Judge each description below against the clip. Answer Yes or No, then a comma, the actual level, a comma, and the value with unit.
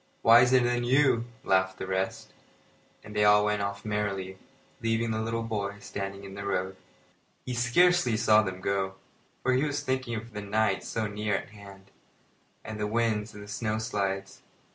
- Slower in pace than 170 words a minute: No, average, 175 wpm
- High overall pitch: No, low, 105 Hz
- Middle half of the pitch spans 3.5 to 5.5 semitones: No, average, 2.7 semitones